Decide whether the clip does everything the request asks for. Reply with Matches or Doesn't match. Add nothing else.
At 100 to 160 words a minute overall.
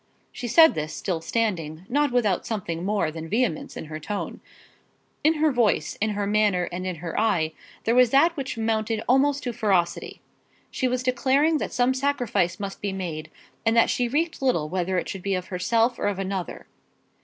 Doesn't match